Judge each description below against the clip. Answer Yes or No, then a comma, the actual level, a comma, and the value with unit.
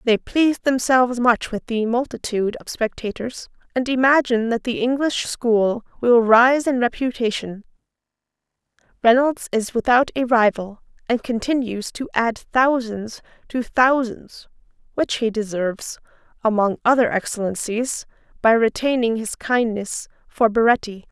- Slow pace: Yes, slow, 120 wpm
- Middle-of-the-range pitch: No, high, 235 Hz